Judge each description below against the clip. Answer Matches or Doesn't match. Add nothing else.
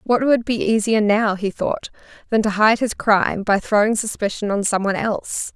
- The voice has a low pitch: Doesn't match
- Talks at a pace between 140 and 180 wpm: Doesn't match